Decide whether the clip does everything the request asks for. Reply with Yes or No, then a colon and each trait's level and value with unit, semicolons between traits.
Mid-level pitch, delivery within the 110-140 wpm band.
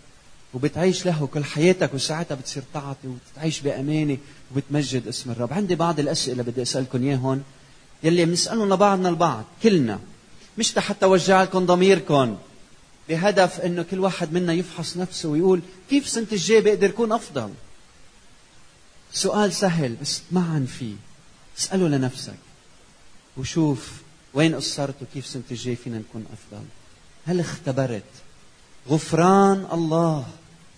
Yes: medium, 155 Hz; average, 120 wpm